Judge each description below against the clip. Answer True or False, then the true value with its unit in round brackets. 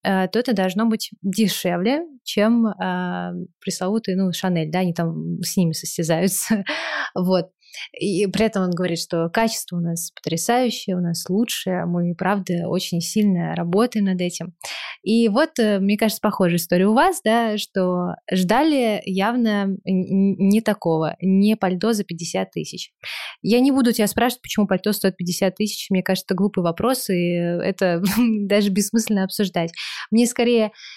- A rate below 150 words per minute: False (155 wpm)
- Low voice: False (195 Hz)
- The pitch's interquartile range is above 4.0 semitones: False (3.5 semitones)